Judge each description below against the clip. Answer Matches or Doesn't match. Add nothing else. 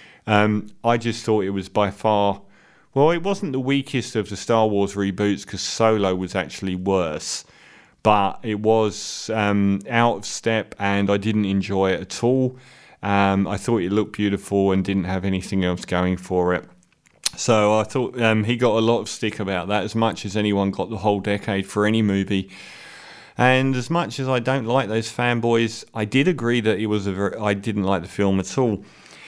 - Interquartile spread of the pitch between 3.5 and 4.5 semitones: Doesn't match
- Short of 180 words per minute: Doesn't match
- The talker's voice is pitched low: Matches